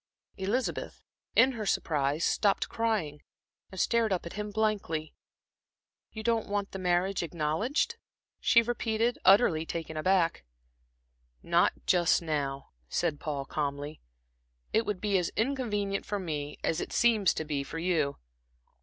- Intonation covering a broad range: Yes, wide, 5.7 semitones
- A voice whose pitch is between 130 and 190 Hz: Yes, medium, 185 Hz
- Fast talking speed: No, slow, 135 wpm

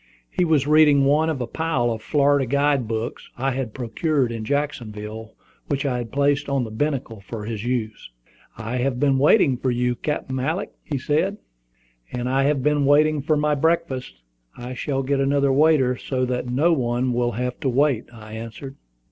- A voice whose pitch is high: No, low, 135 Hz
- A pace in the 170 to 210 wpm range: Yes, average, 185 wpm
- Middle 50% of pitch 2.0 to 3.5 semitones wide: Yes, average, 3.2 semitones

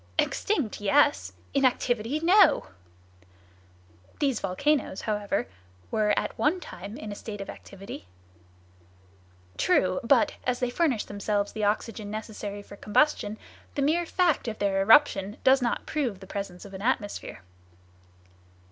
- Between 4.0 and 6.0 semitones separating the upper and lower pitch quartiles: Yes, average, 4.9 semitones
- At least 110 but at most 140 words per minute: Yes, slow, 135 wpm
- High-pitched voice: Yes, high, 215 Hz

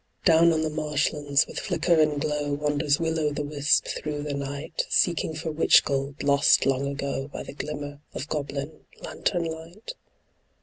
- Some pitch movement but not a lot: No, narrow, 2.0 semitones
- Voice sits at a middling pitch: Yes, medium, 150 Hz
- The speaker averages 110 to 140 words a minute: No, average, 170 wpm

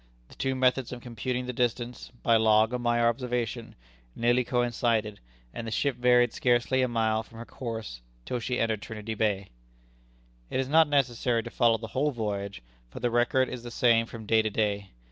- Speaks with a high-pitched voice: No, low, 120 Hz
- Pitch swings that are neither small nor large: No, narrow, 2.0 semitones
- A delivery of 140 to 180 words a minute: No, average, 190 wpm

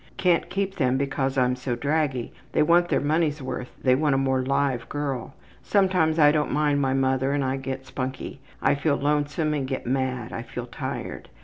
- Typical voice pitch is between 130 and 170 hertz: Yes, medium, 140 Hz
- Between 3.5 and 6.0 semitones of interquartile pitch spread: No, narrow, 2.4 semitones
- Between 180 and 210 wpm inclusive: Yes, average, 195 wpm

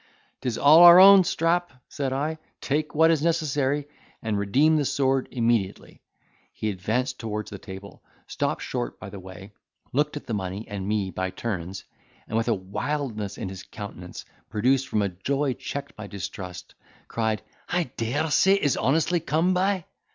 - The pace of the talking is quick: No, average, 165 wpm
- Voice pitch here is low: Yes, low, 125 Hz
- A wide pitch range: Yes, wide, 6.9 semitones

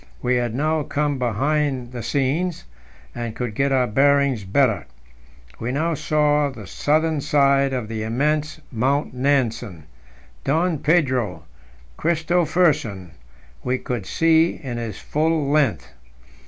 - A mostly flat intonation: No, average, 4.0 semitones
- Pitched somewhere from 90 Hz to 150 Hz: Yes, medium, 140 Hz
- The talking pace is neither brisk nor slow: No, slow, 125 wpm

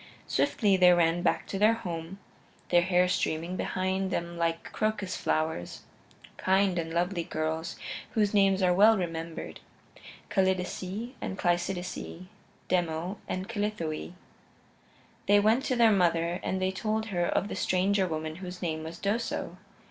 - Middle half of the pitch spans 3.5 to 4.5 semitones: No, average, 2.7 semitones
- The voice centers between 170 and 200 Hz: Yes, medium, 185 Hz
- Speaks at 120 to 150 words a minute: Yes, average, 140 wpm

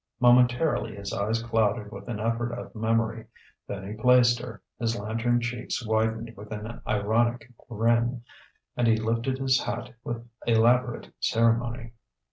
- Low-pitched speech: Yes, low, 115 Hz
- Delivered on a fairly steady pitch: Yes, narrow, 1.5 semitones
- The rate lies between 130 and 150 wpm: Yes, average, 140 wpm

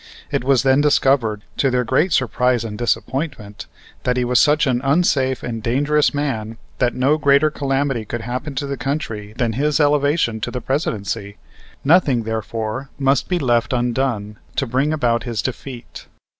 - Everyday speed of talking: Yes, average, 165 wpm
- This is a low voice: Yes, low, 130 Hz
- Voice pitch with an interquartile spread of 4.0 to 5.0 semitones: No, average, 3.5 semitones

